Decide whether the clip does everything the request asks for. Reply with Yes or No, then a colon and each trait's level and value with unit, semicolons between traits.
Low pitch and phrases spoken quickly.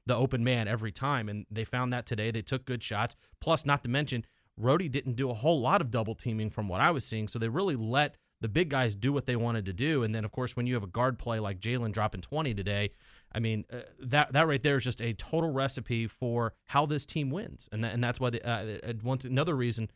Yes: low, 120 Hz; fast, 260 wpm